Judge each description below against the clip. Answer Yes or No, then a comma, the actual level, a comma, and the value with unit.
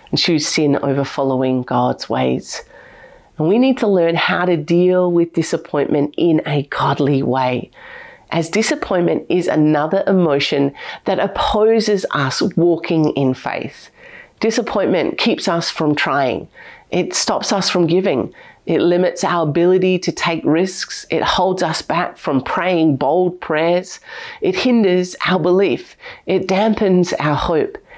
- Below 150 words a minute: Yes, average, 140 wpm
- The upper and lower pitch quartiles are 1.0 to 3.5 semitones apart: No, average, 4.4 semitones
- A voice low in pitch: No, medium, 175 Hz